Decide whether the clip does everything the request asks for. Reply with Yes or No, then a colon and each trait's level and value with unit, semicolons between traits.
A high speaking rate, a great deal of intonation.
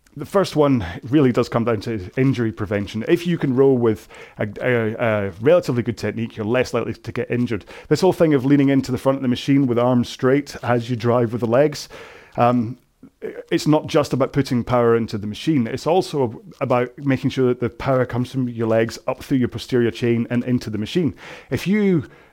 No: fast, 215 wpm; average, 2.8 semitones